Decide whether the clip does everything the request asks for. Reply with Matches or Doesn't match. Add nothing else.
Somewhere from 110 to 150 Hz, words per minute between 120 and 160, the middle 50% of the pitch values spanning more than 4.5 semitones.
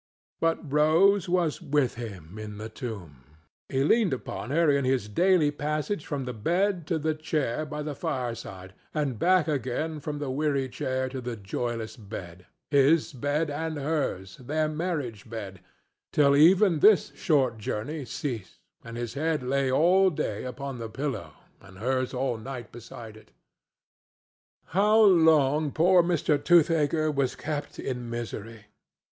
Matches